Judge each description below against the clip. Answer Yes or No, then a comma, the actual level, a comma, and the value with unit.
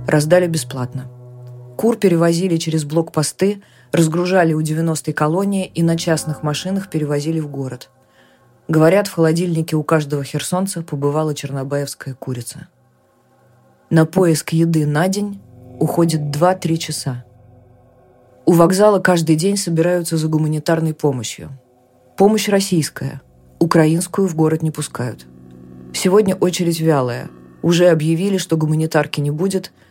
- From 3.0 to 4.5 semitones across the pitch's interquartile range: Yes, average, 4.2 semitones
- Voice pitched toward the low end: No, medium, 155 Hz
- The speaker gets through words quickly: No, average, 115 wpm